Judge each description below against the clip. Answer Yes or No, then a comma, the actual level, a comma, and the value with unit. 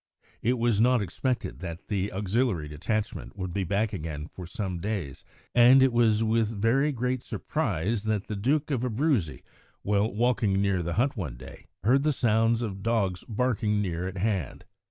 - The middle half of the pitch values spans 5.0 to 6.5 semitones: No, average, 4.2 semitones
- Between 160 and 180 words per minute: Yes, average, 175 wpm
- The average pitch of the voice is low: Yes, low, 105 Hz